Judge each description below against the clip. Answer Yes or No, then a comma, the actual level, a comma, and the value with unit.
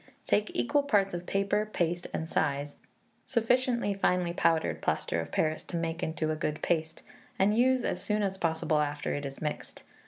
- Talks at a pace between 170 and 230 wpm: Yes, average, 180 wpm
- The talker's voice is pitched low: No, medium, 175 Hz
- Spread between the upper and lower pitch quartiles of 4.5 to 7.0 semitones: Yes, average, 5.0 semitones